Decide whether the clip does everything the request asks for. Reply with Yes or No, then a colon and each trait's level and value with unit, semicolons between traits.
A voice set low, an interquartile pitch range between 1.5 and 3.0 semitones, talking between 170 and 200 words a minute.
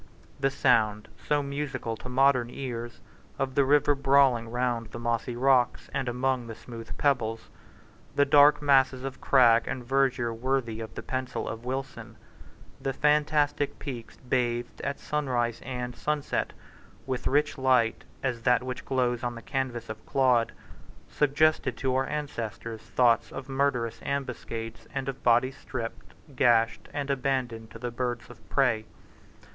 No: low, 125 Hz; narrow, 2.6 semitones; average, 150 wpm